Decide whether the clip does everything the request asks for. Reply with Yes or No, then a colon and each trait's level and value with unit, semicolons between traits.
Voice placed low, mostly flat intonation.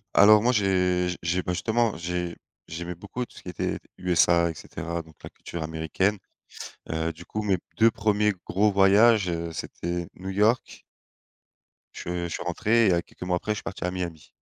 No: very low, 90 Hz; average, 3.5 semitones